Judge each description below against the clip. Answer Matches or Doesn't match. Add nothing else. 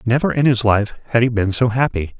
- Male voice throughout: Matches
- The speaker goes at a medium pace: Doesn't match